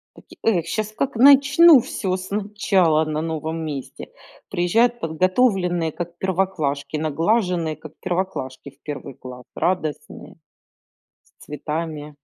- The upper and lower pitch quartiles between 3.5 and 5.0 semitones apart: Yes, average, 4.2 semitones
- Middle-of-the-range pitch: Yes, medium, 175 Hz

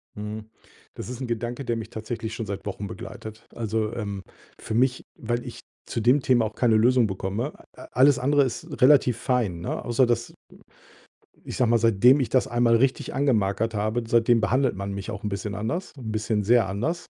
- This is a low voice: Yes, low, 115 Hz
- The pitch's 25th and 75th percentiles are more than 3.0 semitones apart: No, average, 2.7 semitones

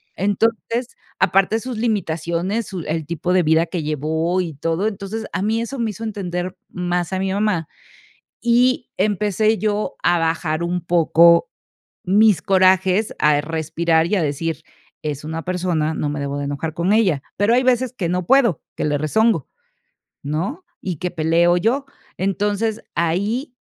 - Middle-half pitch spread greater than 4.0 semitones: Yes, average, 4.7 semitones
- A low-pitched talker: No, medium, 180 Hz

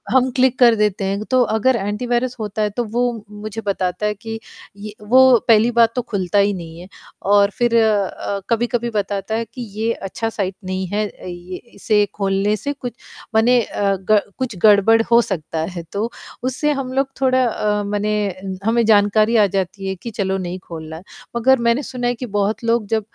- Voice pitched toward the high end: Yes, high, 215 Hz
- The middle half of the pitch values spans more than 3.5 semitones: No, average, 3.2 semitones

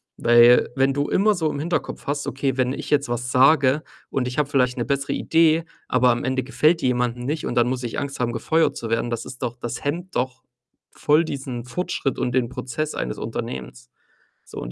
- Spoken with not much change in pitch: No, average, 3.0 semitones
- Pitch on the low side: Yes, low, 130 Hz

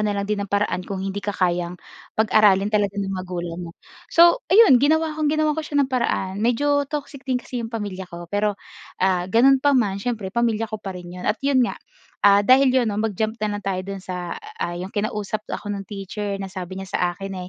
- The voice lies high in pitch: Yes, high, 205 Hz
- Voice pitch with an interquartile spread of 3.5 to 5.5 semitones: Yes, average, 4.3 semitones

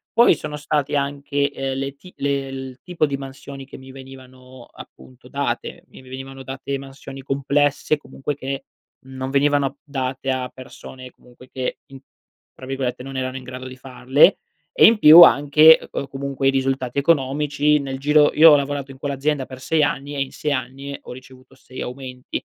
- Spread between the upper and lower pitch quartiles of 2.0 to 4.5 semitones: No, narrow, 1.5 semitones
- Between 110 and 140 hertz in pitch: Yes, low, 135 Hz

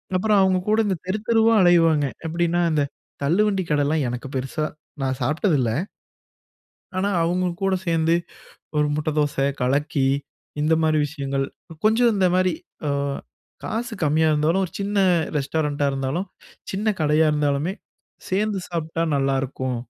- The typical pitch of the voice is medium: Yes, medium, 160 Hz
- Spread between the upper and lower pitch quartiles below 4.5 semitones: No, average, 4.8 semitones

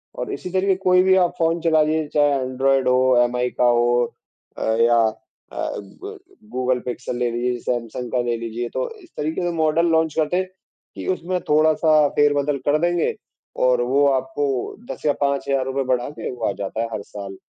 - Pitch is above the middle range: No, medium, 140 Hz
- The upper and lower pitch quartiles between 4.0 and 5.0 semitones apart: Yes, average, 4.4 semitones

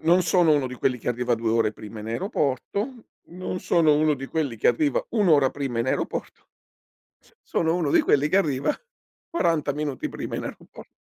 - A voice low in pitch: No, medium, 145 Hz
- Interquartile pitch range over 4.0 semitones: Yes, average, 5.1 semitones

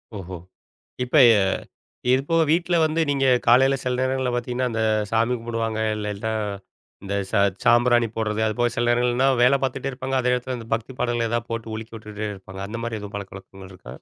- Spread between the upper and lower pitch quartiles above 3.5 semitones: No, average, 2.8 semitones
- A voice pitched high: No, low, 120 Hz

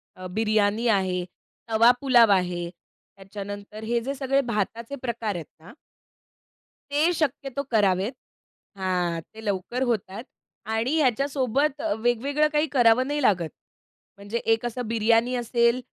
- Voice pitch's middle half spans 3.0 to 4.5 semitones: Yes, average, 4.2 semitones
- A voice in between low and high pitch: No, high, 230 Hz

